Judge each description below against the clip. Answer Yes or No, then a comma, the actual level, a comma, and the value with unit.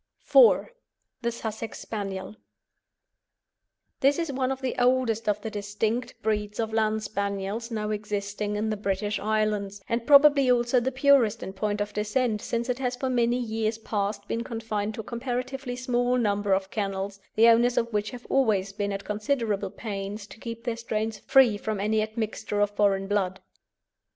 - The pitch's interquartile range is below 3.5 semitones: Yes, average, 2.8 semitones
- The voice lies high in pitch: Yes, high, 220 Hz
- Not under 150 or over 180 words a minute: Yes, average, 170 wpm